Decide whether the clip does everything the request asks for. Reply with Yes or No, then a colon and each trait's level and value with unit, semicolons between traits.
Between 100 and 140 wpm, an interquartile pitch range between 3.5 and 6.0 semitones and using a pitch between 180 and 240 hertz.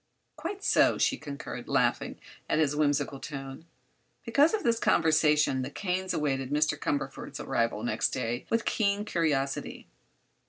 No: slow, 135 wpm; average, 5.2 semitones; medium, 150 Hz